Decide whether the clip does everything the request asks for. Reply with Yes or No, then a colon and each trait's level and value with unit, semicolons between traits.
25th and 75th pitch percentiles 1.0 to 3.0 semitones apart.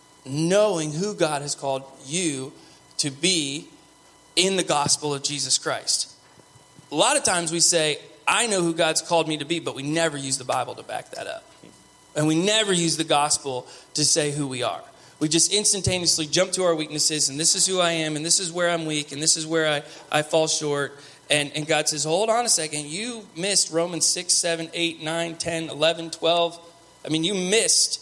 Yes: narrow, 2.4 semitones